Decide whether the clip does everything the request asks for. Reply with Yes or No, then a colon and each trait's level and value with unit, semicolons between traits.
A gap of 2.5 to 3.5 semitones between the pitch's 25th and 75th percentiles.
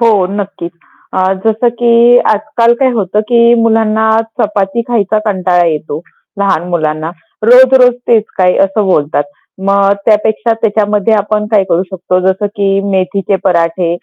Yes: average, 3.2 semitones